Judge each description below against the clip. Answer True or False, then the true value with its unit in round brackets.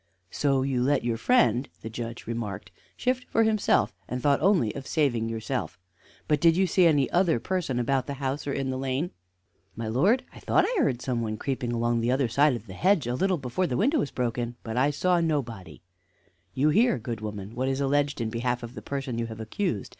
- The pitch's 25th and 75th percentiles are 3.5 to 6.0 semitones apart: True (4.5 semitones)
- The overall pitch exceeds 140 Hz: False (130 Hz)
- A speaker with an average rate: False (220 wpm)